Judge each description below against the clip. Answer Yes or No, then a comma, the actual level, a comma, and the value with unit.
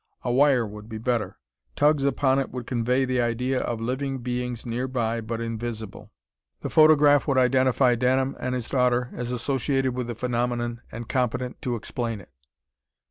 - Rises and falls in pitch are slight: Yes, narrow, 1.9 semitones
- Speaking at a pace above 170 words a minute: No, average, 165 wpm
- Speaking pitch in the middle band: No, low, 125 Hz